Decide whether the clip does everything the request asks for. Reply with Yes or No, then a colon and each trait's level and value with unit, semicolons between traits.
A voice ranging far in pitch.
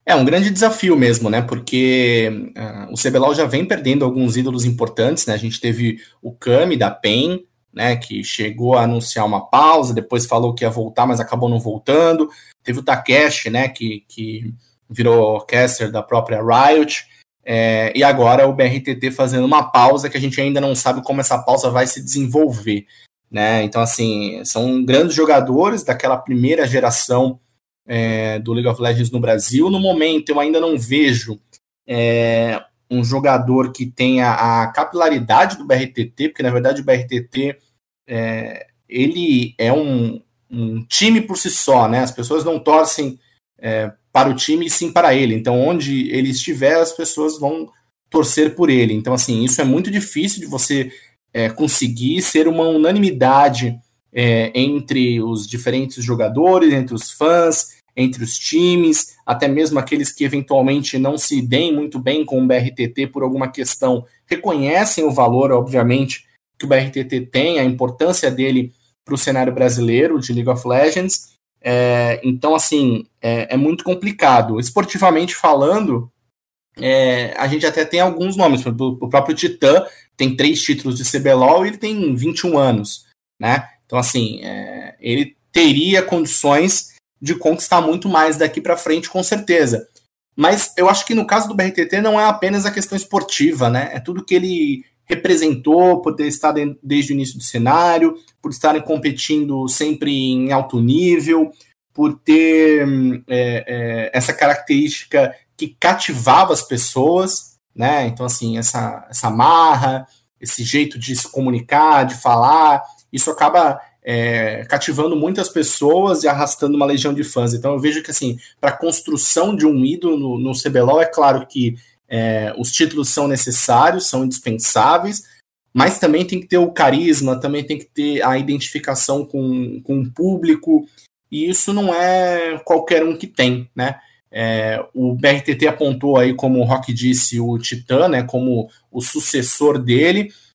No: average, 4.5 semitones